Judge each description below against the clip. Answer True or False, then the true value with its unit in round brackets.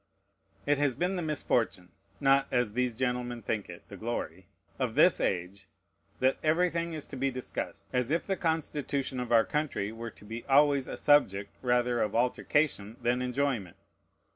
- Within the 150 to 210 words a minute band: True (165 wpm)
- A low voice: True (125 Hz)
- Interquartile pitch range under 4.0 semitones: False (4.4 semitones)